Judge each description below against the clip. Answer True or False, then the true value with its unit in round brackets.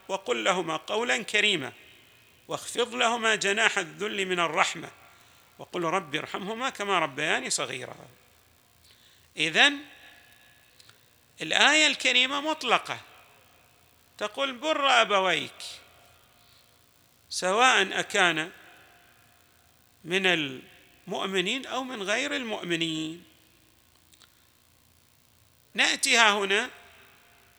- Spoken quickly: False (70 wpm)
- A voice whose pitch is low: False (190 Hz)